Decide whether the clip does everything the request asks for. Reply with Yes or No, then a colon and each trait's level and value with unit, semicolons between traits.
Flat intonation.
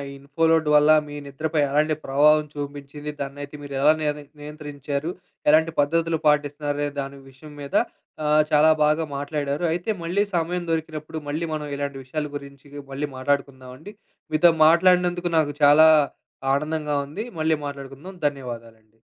Yes: narrow, 2.0 semitones